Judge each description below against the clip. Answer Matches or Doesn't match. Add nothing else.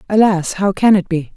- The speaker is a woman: Matches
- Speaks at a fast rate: Matches